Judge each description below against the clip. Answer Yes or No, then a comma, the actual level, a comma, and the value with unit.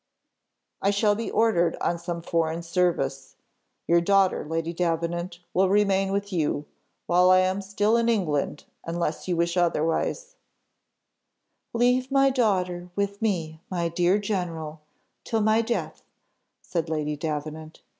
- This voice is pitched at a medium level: Yes, medium, 180 Hz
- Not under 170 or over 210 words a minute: No, slow, 135 wpm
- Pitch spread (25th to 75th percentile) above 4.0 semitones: No, average, 3.5 semitones